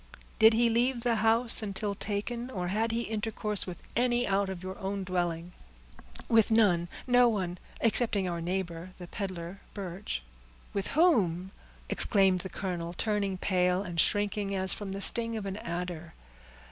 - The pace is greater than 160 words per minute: No, average, 155 wpm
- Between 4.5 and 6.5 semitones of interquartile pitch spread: No, average, 3.6 semitones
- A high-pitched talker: Yes, high, 195 Hz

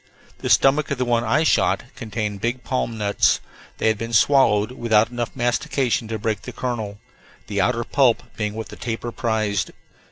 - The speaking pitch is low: Yes, low, 115 Hz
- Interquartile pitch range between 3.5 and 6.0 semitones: No, narrow, 2.5 semitones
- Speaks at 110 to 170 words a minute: No, average, 180 wpm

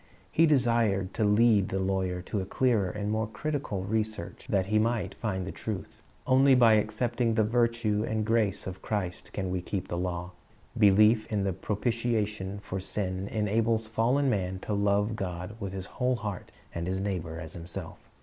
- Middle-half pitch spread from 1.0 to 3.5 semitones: Yes, average, 3.1 semitones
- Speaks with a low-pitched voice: Yes, low, 105 Hz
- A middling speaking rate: Yes, average, 175 wpm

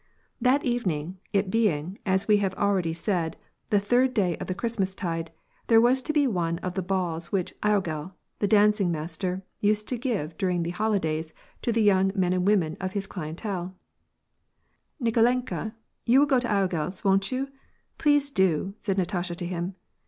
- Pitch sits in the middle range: No, high, 195 Hz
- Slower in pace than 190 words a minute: Yes, average, 175 wpm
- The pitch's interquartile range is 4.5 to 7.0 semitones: No, average, 3.8 semitones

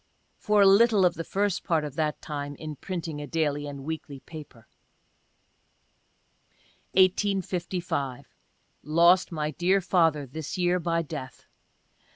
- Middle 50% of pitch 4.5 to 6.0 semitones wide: No, average, 3.8 semitones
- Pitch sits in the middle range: Yes, medium, 165 Hz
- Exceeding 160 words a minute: No, slow, 135 wpm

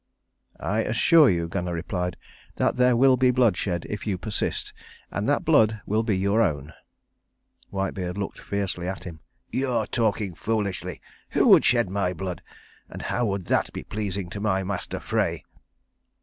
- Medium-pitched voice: No, low, 100 Hz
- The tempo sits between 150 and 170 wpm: Yes, average, 165 wpm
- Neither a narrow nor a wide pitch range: Yes, average, 3.6 semitones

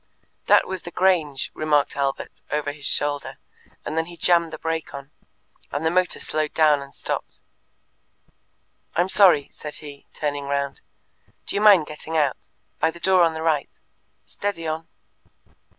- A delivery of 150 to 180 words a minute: Yes, average, 160 wpm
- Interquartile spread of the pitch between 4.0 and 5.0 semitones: No, average, 2.9 semitones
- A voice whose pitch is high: No, medium, 155 Hz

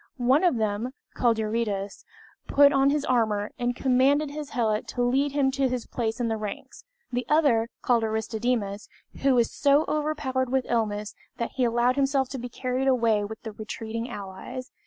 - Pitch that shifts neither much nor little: Yes, average, 3.3 semitones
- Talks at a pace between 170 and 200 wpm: Yes, average, 175 wpm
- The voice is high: Yes, high, 245 Hz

